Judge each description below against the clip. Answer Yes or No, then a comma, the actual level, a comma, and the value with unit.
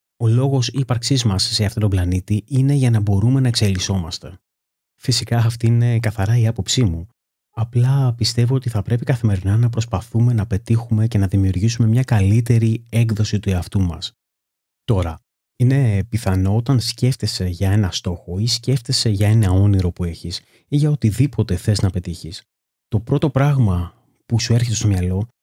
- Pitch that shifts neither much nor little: Yes, average, 4.0 semitones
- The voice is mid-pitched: No, low, 110 Hz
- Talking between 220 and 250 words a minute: No, average, 165 wpm